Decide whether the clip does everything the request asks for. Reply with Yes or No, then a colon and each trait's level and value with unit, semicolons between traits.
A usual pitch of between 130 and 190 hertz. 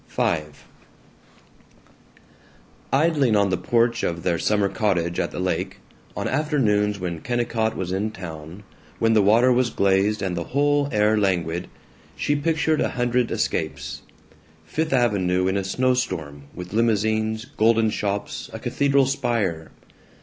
No: low, 105 Hz